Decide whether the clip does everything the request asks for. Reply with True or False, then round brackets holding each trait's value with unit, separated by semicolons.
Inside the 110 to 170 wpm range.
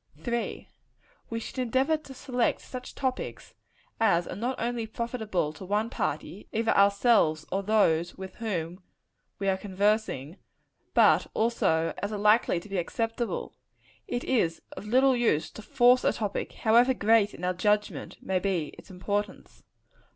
True (155 wpm)